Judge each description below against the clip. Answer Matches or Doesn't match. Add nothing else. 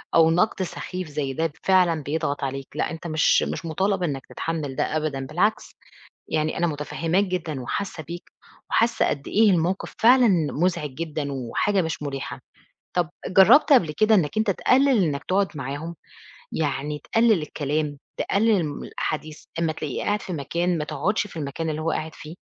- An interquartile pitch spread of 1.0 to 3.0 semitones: Doesn't match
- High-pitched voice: Doesn't match